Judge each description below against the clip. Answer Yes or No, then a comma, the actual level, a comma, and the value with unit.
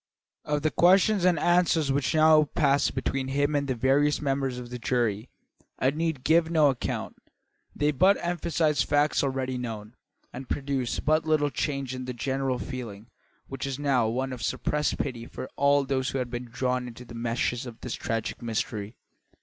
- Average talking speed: Yes, average, 175 wpm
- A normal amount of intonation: Yes, average, 3.2 semitones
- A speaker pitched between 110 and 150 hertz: Yes, low, 135 Hz